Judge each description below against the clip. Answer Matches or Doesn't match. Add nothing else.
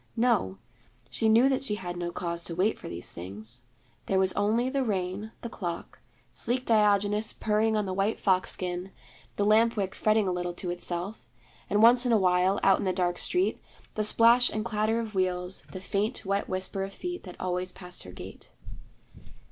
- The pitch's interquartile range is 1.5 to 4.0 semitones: Matches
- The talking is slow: Doesn't match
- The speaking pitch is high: Matches